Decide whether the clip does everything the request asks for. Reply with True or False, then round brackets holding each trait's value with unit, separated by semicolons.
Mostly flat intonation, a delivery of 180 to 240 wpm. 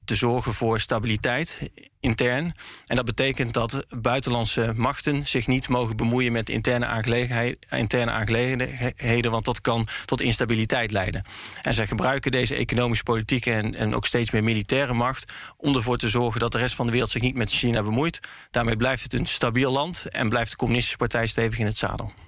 True (1.8 semitones; 185 wpm)